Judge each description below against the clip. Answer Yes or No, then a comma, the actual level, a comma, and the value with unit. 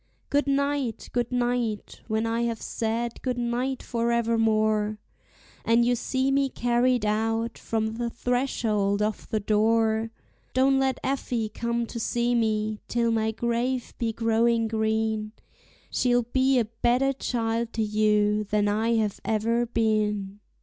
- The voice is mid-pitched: No, high, 230 Hz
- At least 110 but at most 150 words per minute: Yes, average, 140 wpm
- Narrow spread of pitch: Yes, narrow, 1.9 semitones